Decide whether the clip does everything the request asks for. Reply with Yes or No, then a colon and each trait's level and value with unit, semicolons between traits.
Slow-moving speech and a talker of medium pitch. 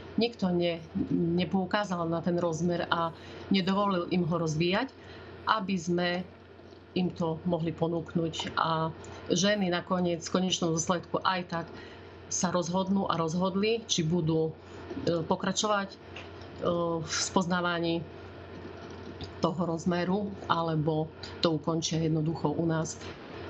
Yes: slow, 105 wpm; medium, 170 Hz